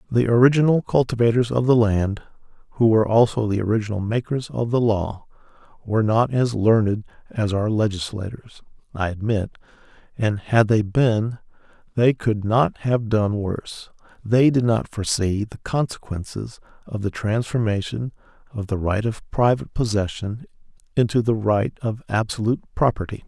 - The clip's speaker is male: Yes, male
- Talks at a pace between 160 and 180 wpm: No, average, 140 wpm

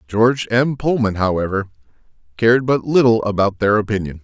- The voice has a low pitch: Yes, low, 110 Hz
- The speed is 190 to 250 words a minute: No, average, 140 wpm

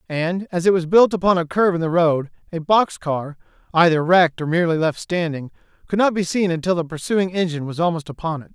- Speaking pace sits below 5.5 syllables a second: No, 6.1 syllables/s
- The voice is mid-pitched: Yes, medium, 170 Hz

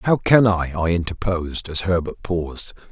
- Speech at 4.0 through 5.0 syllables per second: Yes, 4.8 syllables/s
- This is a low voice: Yes, very low, 90 Hz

